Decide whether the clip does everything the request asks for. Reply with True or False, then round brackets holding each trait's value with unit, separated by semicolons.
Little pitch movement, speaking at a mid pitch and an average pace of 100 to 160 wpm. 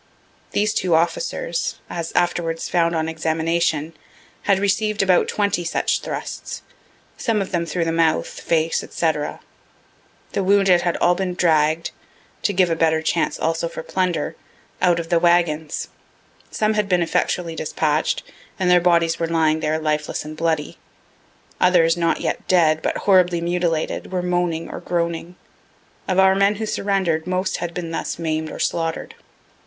True (2.0 semitones; 170 Hz; 155 wpm)